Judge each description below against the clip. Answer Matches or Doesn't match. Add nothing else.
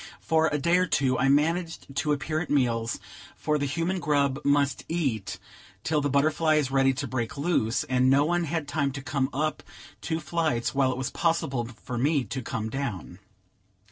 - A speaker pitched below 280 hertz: Matches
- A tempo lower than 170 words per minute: Doesn't match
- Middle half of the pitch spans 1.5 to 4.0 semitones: Matches